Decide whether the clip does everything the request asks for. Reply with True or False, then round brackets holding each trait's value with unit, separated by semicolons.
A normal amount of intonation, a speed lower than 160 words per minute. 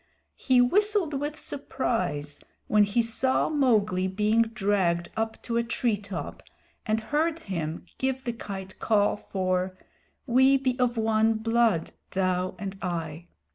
True (5.0 semitones; 135 wpm)